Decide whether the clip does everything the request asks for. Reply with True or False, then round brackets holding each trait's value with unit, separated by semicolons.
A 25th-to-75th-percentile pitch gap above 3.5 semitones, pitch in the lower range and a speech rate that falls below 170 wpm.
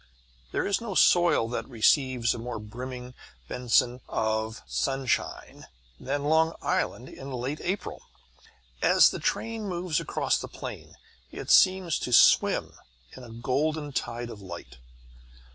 True (5.1 semitones; 130 Hz; 135 wpm)